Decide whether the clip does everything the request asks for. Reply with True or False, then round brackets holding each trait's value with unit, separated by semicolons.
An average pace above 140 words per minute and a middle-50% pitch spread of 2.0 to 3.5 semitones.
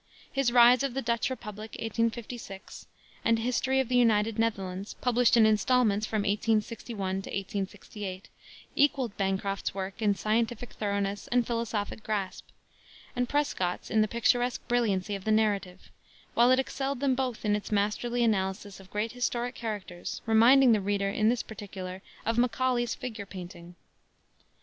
True (150 wpm; 3.2 semitones)